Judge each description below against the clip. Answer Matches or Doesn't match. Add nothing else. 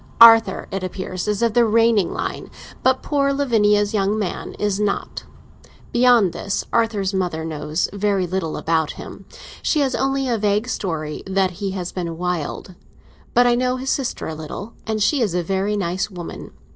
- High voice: Matches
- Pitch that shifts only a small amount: Doesn't match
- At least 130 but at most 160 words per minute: Doesn't match